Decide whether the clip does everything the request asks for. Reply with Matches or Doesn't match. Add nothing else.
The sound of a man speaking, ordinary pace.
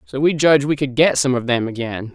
Doesn't match